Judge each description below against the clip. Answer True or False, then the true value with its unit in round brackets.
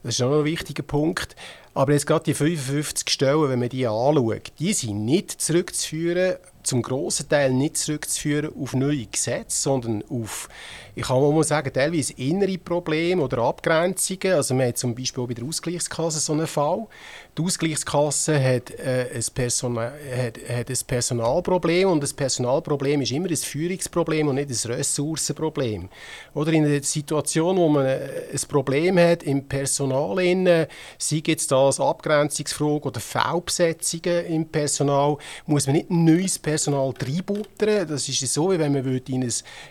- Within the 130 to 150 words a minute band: False (160 wpm)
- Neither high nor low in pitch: True (150 Hz)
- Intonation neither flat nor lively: True (3.7 semitones)